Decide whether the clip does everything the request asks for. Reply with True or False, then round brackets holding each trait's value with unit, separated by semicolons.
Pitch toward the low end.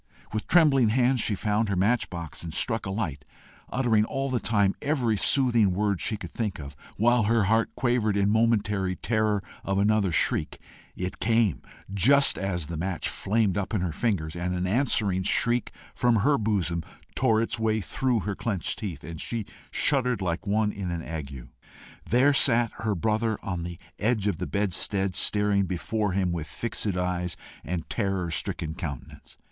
True (105 Hz)